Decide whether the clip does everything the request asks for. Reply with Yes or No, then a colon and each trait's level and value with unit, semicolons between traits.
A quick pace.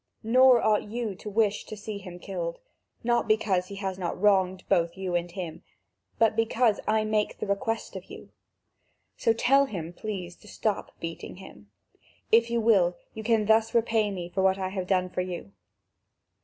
No: average, 185 wpm